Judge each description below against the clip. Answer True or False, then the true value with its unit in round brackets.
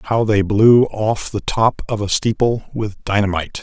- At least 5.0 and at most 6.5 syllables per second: False (4.6 syllables/s)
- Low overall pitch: True (105 Hz)